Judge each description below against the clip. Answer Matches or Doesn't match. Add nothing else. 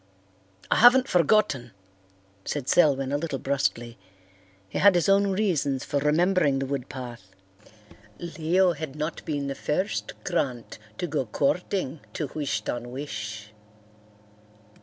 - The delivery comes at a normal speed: Doesn't match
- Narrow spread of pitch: Doesn't match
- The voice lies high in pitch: Doesn't match